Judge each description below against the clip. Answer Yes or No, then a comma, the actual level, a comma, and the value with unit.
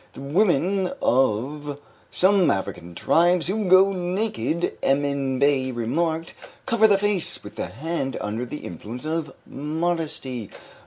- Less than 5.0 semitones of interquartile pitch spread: No, wide, 5.4 semitones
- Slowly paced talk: Yes, slow, 125 wpm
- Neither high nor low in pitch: Yes, medium, 150 Hz